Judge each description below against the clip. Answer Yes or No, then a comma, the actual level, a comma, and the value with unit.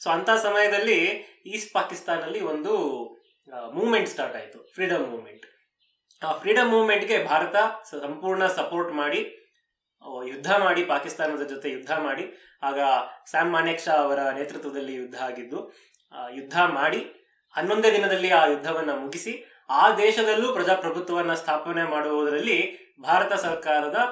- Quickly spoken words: Yes, fast, 115 wpm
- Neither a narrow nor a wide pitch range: No, wide, 6.6 semitones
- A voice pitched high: No, medium, 170 Hz